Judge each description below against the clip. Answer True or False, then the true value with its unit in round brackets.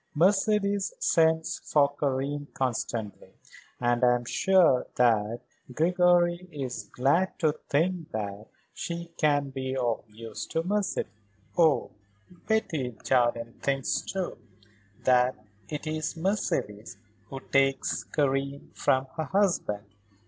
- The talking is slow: True (110 wpm)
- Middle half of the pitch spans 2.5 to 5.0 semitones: False (5.6 semitones)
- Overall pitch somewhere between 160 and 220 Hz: False (140 Hz)